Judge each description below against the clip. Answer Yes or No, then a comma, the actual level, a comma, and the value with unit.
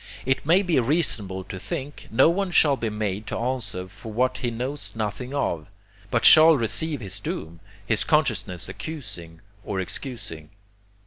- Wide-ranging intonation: Yes, wide, 6.8 semitones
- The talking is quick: No, average, 155 wpm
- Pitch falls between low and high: No, low, 120 Hz